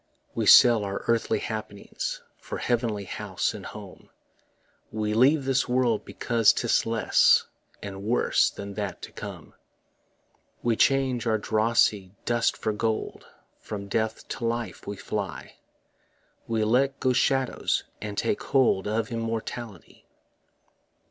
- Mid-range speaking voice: No, low, 115 Hz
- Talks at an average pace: No, slow, 130 wpm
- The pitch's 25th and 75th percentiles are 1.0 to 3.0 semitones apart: Yes, narrow, 2.5 semitones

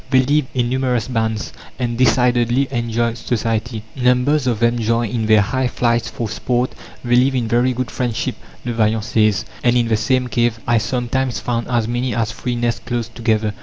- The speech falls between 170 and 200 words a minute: Yes, average, 190 wpm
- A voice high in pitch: No, low, 120 Hz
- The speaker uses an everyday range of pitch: No, narrow, 1.7 semitones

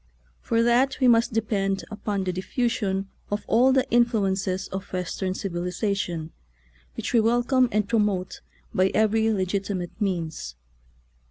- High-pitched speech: Yes, high, 205 Hz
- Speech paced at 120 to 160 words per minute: Yes, average, 140 wpm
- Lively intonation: No, average, 3.6 semitones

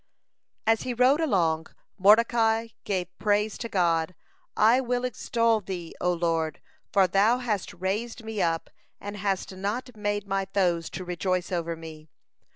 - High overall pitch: Yes, high, 195 Hz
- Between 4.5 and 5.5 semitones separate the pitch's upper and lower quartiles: No, average, 4.1 semitones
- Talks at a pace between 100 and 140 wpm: No, average, 155 wpm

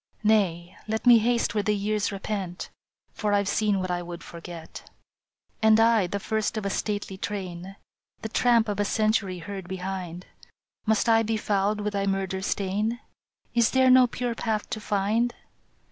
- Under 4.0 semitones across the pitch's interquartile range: Yes, narrow, 2.5 semitones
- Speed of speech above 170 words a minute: Yes, average, 180 wpm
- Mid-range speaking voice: No, high, 205 Hz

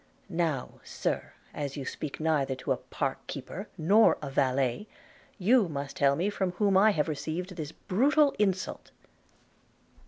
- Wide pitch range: Yes, wide, 6.0 semitones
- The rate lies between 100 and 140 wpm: No, average, 150 wpm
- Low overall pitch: No, medium, 160 Hz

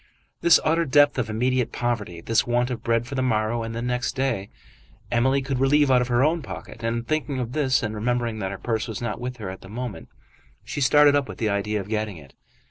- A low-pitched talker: Yes, low, 120 Hz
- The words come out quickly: Yes, fast, 235 wpm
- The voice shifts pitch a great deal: No, average, 3.3 semitones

